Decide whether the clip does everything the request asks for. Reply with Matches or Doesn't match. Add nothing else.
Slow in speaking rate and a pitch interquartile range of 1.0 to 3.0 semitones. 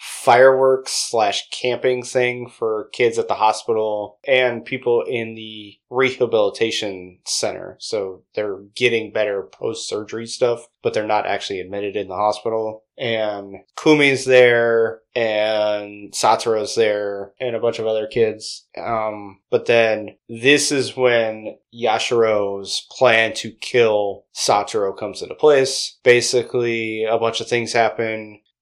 Matches